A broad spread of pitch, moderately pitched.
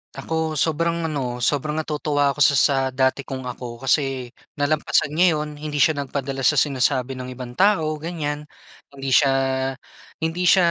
No: average, 2.7 semitones; medium, 145 Hz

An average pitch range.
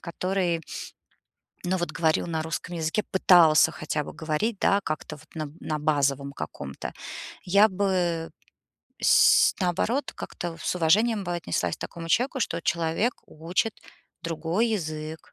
Yes: average, 3.3 semitones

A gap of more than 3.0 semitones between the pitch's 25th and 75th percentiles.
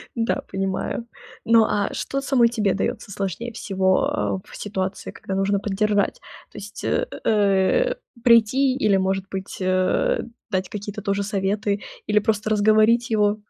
No: narrow, 2.6 semitones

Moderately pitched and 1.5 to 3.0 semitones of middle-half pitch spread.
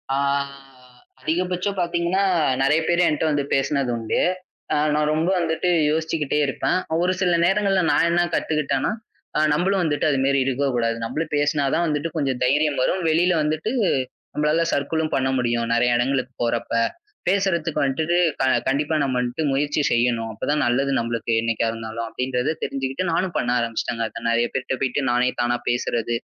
No: medium, 145 Hz; average, 4.8 semitones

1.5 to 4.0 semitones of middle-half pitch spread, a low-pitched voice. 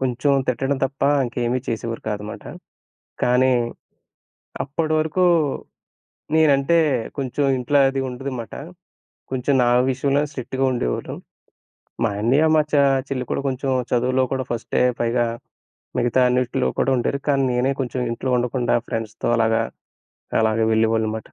Yes: narrow, 2.6 semitones; low, 125 Hz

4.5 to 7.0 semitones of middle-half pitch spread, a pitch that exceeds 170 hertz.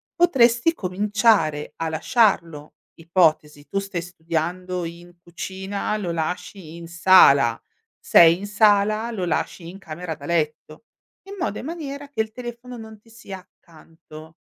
Yes: average, 4.9 semitones; medium, 185 Hz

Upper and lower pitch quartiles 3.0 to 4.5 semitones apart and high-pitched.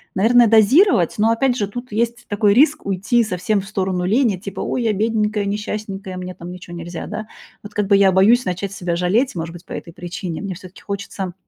Yes: average, 3.3 semitones; high, 200 Hz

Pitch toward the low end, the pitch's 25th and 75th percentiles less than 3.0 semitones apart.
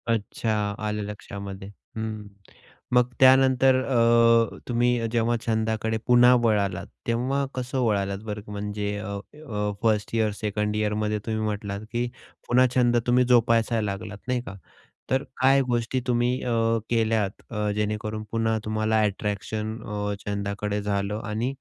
Yes: low, 110 Hz; narrow, 2.5 semitones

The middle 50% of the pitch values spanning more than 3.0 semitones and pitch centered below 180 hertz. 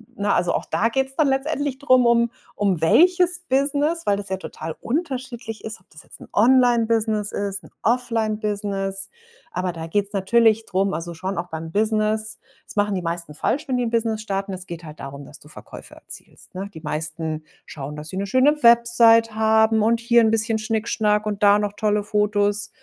No: average, 3.4 semitones; high, 215 Hz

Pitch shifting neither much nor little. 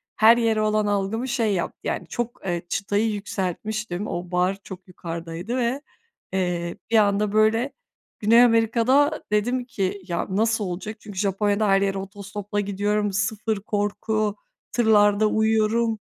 No: narrow, 2.3 semitones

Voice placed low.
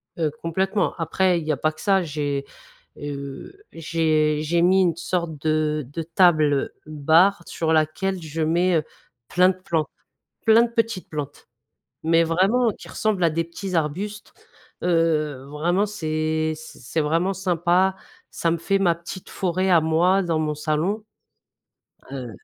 No: medium, 165 Hz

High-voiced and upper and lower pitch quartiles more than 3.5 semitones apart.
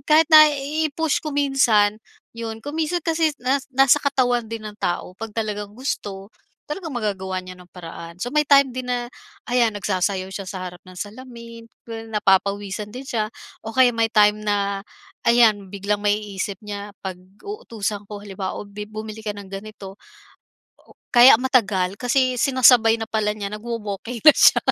Yes: high, 215 Hz; average, 4.2 semitones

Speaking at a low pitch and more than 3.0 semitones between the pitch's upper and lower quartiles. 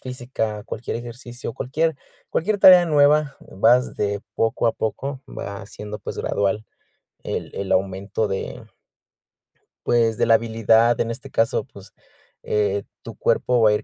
Yes: low, 115 Hz; average, 3.4 semitones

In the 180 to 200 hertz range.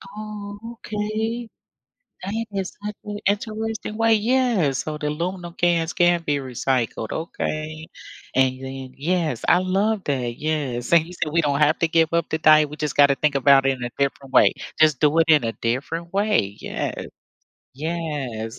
No: medium, 155 Hz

